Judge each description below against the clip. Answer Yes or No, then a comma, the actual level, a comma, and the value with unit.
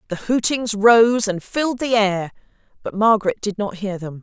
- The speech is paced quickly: No, average, 170 wpm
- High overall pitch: Yes, high, 215 Hz